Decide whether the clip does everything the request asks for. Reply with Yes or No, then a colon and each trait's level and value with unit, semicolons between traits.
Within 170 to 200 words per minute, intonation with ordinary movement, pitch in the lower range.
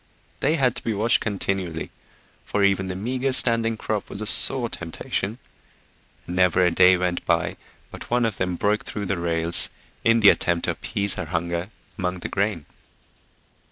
Yes: average, 175 wpm; average, 3.8 semitones; low, 100 Hz